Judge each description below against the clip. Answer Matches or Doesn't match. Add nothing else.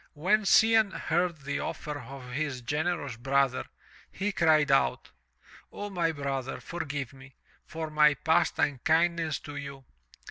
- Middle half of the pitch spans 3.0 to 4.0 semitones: Matches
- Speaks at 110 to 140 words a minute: Matches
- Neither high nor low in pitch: Matches